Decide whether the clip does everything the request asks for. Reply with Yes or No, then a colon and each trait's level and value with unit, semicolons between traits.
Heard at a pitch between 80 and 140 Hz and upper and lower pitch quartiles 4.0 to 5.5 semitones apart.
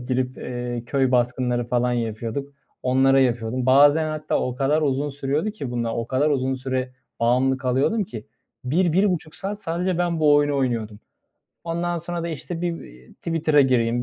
Yes: low, 135 Hz; average, 4.3 semitones